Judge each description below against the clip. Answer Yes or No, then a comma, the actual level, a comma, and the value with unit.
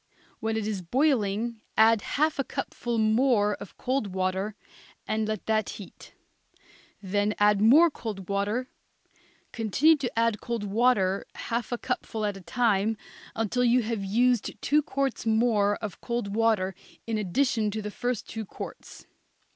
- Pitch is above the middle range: Yes, high, 220 Hz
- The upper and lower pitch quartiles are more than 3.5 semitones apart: No, average, 2.9 semitones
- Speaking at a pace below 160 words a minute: Yes, average, 150 wpm